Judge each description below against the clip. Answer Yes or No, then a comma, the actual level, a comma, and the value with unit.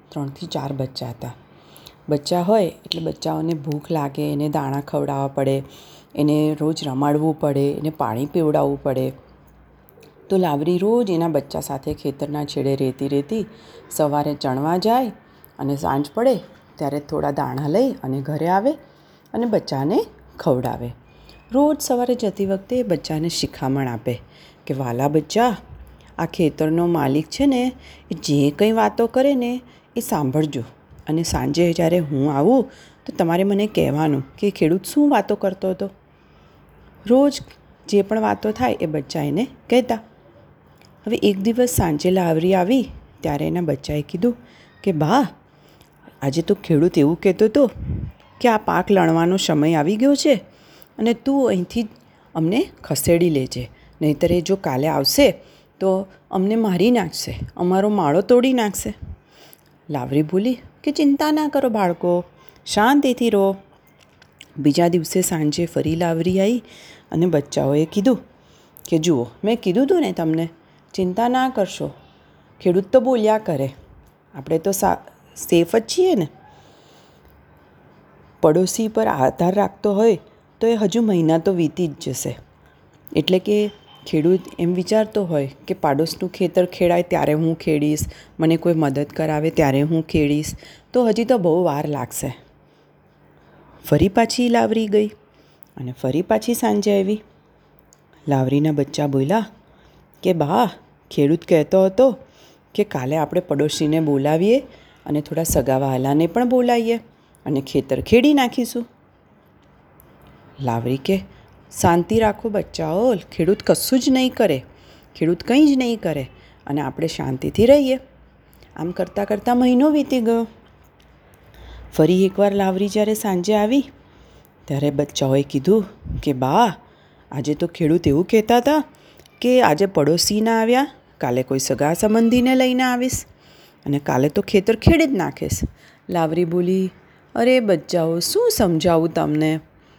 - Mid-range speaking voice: Yes, medium, 170 Hz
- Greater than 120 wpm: Yes, average, 135 wpm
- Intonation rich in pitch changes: Yes, wide, 6.8 semitones